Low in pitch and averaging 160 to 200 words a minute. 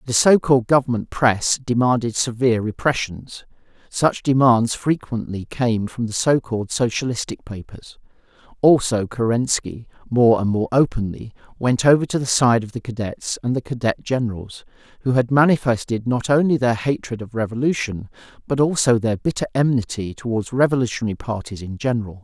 No: low, 120 Hz; average, 145 wpm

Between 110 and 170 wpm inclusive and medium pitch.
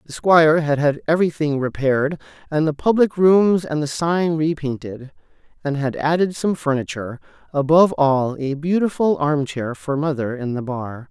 Yes: average, 150 wpm; medium, 150 Hz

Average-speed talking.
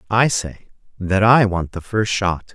Yes: average, 190 wpm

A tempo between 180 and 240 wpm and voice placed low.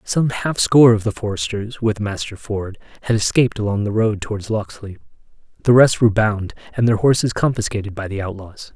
Yes: average, 185 wpm; low, 110 Hz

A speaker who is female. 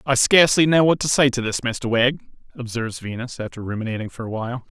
No: male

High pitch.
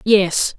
Yes: high, 200 Hz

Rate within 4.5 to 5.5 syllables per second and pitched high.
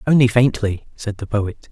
No: 4.8 syllables/s; low, 110 Hz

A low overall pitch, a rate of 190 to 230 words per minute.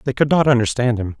No: low, 125 Hz; fast, 250 wpm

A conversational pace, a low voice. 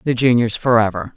Yes: average, 155 wpm; low, 115 Hz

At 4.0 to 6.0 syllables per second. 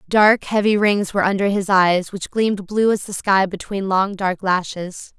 Yes: 4.6 syllables/s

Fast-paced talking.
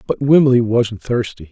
No: average, 160 wpm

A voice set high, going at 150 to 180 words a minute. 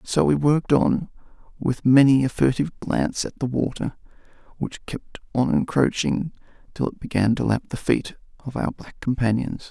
No: low, 135 Hz; average, 165 wpm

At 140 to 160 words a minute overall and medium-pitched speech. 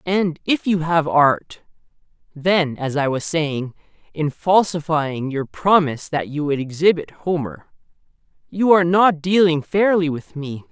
Yes: average, 145 wpm; medium, 160 Hz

